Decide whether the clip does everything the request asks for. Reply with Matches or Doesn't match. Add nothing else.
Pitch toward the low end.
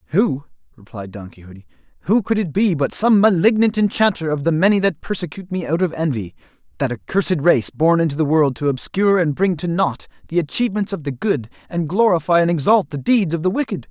Doesn't match